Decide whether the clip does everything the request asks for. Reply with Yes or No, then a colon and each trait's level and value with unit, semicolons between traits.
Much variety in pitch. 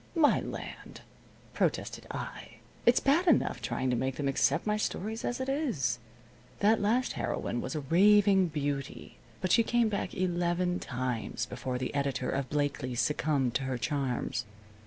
Yes: wide, 8.3 semitones